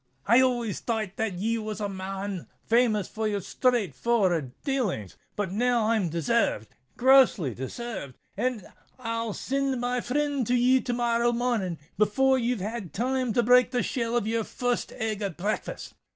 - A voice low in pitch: No, high, 230 Hz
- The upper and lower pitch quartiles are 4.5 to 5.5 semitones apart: No, average, 3.7 semitones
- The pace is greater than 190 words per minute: No, average, 150 wpm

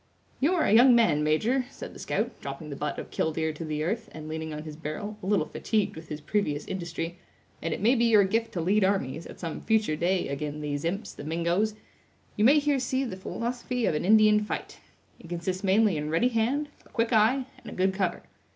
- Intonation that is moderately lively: No, wide, 6.0 semitones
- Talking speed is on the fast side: Yes, fast, 225 wpm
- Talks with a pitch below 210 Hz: Yes, high, 190 Hz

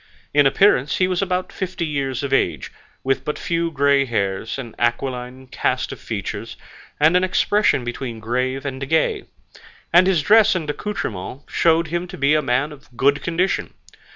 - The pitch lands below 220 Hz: Yes, medium, 140 Hz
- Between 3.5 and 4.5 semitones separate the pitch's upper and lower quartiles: No, average, 5.1 semitones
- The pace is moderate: Yes, average, 170 wpm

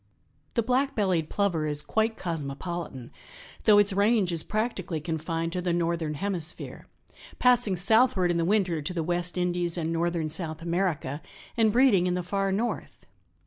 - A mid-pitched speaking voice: Yes, medium, 175 Hz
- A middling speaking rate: Yes, average, 160 wpm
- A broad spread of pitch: No, average, 3.6 semitones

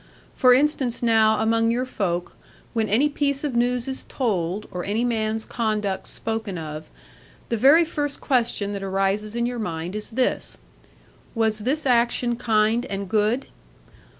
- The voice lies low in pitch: No, high, 225 Hz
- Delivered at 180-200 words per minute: No, average, 150 wpm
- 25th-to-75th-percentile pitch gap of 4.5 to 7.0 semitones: No, average, 3.1 semitones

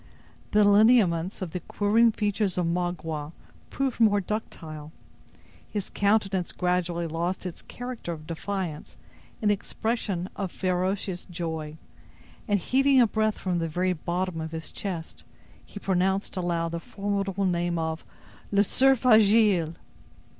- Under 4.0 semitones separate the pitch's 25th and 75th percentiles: Yes, average, 3.4 semitones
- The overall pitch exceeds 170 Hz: Yes, medium, 185 Hz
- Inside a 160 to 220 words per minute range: No, slow, 135 wpm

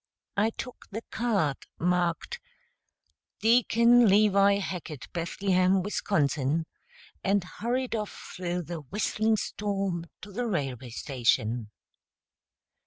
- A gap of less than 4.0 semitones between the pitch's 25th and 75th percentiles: No, average, 4.6 semitones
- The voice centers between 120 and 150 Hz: No, high, 190 Hz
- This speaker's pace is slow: Yes, slow, 100 wpm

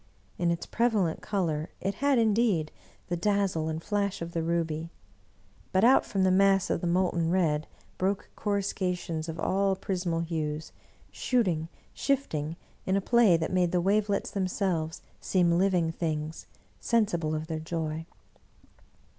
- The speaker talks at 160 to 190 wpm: No, average, 145 wpm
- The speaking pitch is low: No, medium, 180 Hz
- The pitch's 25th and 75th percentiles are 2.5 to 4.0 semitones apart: Yes, average, 3.5 semitones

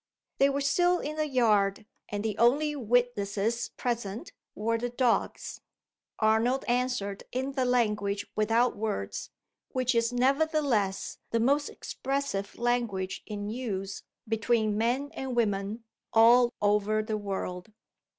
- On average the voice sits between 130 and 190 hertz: No, high, 230 Hz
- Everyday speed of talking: No, slow, 125 wpm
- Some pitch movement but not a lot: Yes, average, 3.5 semitones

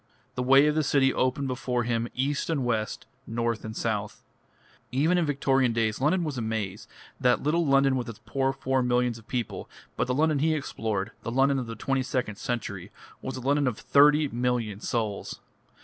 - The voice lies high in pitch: No, low, 125 Hz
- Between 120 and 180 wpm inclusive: No, average, 195 wpm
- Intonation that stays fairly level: No, average, 3.3 semitones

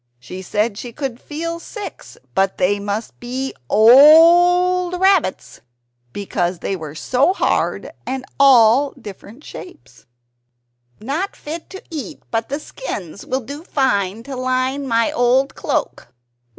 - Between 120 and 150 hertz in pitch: No, very high, 255 Hz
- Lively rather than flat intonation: Yes, wide, 6.5 semitones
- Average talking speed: No, slow, 130 wpm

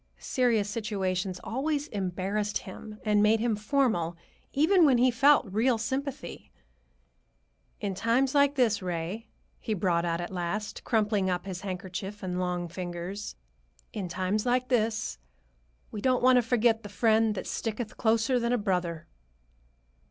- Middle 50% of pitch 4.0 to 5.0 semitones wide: Yes, average, 4.6 semitones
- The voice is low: No, high, 210 Hz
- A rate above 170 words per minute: No, average, 145 wpm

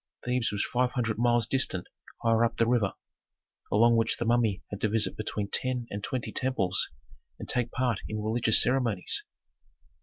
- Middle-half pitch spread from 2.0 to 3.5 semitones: Yes, narrow, 2.4 semitones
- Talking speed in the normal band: Yes, average, 170 wpm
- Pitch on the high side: No, low, 115 Hz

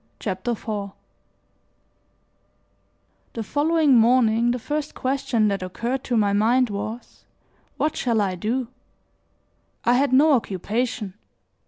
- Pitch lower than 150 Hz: No, high, 235 Hz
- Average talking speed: No, slow, 115 wpm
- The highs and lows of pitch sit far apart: No, average, 3.7 semitones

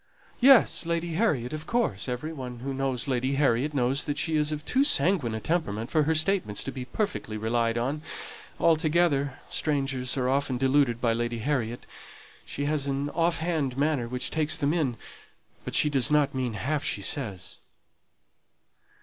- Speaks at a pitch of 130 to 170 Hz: Yes, medium, 140 Hz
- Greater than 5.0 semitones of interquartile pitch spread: No, average, 4.0 semitones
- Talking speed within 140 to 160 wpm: No, average, 170 wpm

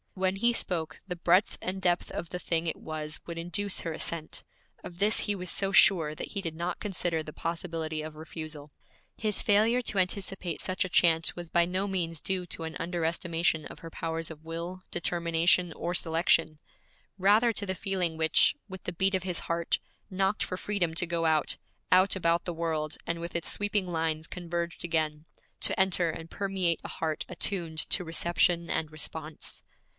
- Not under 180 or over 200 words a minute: Yes, average, 190 wpm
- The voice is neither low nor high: Yes, medium, 170 Hz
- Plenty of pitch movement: No, narrow, 2.5 semitones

